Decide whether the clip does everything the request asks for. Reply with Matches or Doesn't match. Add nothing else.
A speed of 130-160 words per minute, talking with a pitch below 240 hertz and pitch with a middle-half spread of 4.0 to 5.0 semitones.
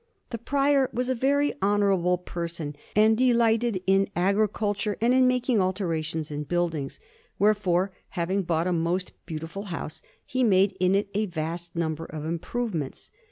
Matches